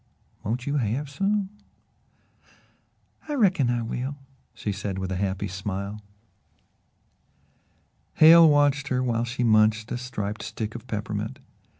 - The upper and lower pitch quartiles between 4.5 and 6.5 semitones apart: Yes, average, 5.3 semitones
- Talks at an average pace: No, slow, 125 wpm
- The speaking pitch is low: Yes, low, 120 Hz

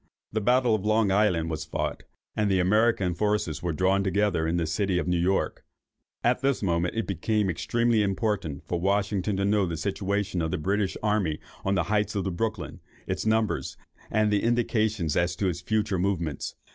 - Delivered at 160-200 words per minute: Yes, average, 185 wpm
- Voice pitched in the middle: No, low, 100 Hz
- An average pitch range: Yes, average, 3.3 semitones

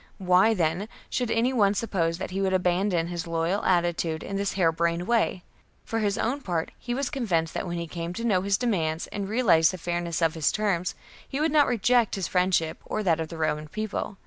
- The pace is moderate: No, fast, 220 wpm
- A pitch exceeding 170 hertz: Yes, medium, 185 Hz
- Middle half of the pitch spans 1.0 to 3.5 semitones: No, average, 4.3 semitones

